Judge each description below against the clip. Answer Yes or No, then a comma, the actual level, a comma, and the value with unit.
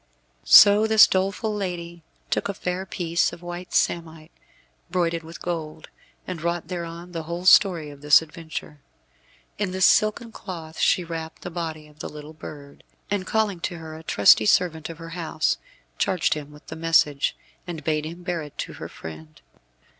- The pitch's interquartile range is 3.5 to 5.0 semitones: No, narrow, 2.4 semitones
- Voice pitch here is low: No, medium, 165 Hz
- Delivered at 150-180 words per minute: Yes, average, 175 wpm